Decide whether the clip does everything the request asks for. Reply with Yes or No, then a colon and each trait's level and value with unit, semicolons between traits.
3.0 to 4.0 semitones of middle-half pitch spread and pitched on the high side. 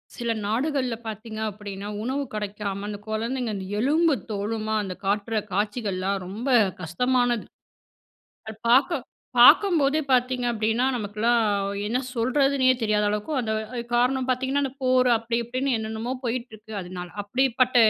Yes: average, 3.4 semitones; high, 230 Hz